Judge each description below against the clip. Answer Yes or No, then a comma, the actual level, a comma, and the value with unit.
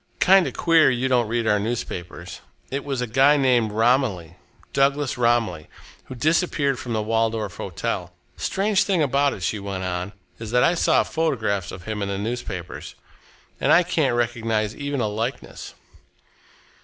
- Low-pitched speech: Yes, low, 120 Hz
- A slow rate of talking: No, average, 165 wpm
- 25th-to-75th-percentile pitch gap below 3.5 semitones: No, average, 4.9 semitones